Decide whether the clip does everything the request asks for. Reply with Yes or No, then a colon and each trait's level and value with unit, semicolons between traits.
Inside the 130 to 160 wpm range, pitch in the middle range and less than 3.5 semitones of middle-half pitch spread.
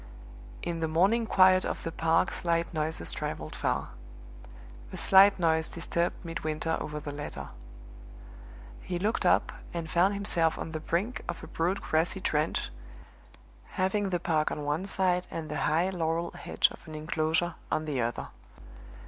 Yes: average, 155 wpm; medium, 165 Hz; average, 2.8 semitones